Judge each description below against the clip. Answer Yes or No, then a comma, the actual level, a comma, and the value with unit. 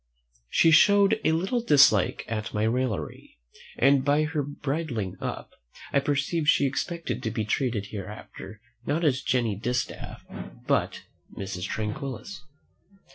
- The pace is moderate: No, slow, 130 wpm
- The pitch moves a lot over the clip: Yes, wide, 6.0 semitones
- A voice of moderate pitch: No, low, 130 Hz